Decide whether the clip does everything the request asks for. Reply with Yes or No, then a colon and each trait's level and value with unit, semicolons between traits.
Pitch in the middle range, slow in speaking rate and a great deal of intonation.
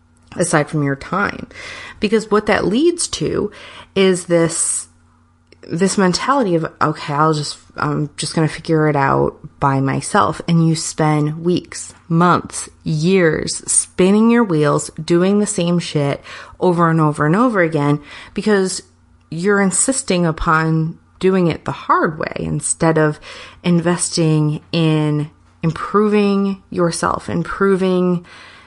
No: medium, 165 Hz; slow, 130 wpm; average, 3.8 semitones